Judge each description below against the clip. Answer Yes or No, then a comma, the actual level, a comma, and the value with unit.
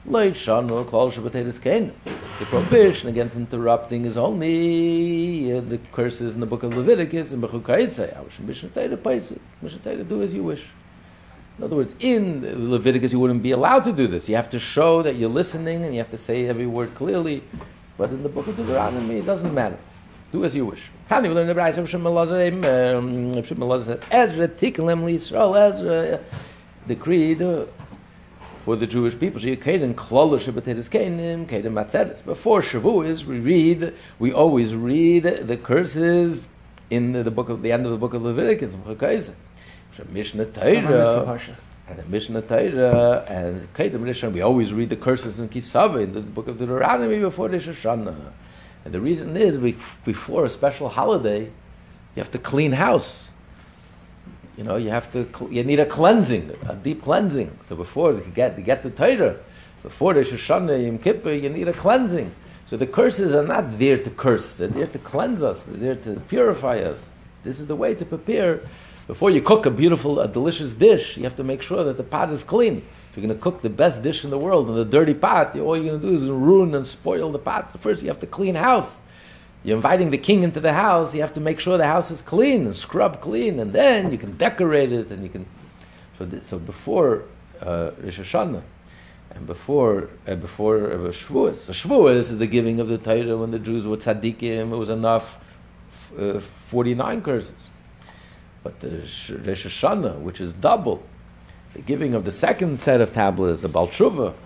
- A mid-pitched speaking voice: No, low, 125 Hz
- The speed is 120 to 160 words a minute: No, average, 195 wpm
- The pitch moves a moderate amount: No, wide, 6.4 semitones